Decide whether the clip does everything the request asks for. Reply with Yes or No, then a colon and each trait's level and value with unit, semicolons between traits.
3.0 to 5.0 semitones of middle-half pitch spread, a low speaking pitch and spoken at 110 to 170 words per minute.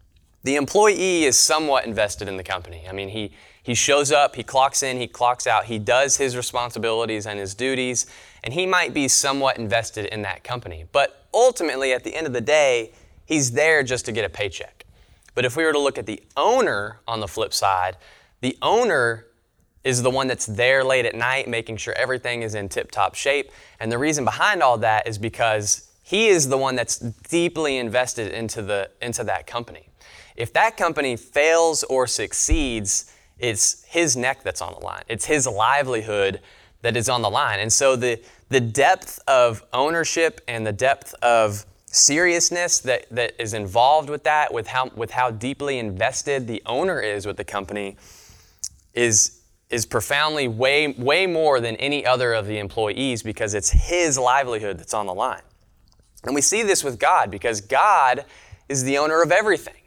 No: average, 4.5 semitones; low, 120 Hz; average, 185 wpm